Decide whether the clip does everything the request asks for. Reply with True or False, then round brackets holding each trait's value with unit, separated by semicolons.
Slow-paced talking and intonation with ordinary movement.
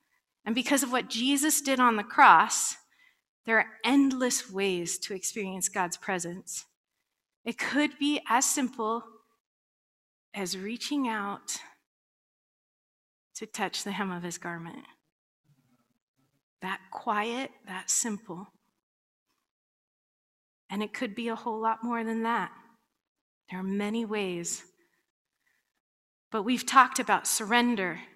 True (115 wpm; 4.4 semitones)